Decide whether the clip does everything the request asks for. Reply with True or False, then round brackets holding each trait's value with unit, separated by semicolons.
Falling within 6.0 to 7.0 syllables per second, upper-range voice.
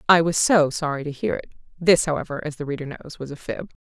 False (6.6 syllables/s; 150 Hz)